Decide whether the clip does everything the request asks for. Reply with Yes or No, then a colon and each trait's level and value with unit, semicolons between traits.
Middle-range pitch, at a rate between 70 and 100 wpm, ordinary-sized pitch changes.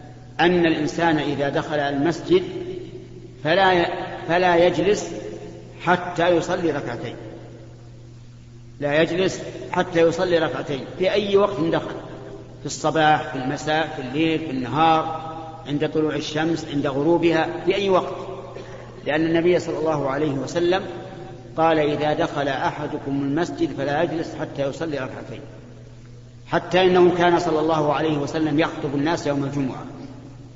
No: medium, 155 Hz; average, 120 wpm; average, 3.7 semitones